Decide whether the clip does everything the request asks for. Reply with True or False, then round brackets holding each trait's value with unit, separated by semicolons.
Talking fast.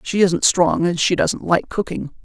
True (215 wpm)